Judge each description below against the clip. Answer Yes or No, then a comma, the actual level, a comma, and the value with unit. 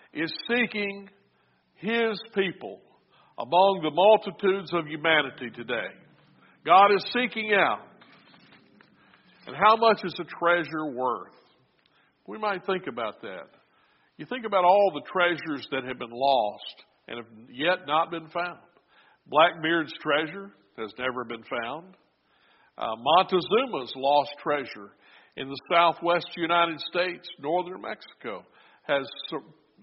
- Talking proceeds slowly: Yes, slow, 125 wpm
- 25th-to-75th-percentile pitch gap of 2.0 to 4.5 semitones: No, average, 5.1 semitones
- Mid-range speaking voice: Yes, medium, 170 Hz